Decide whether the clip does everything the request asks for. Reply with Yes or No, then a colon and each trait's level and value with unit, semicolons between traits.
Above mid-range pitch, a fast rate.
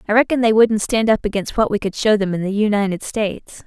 Yes: high, 210 Hz; fast, 280 wpm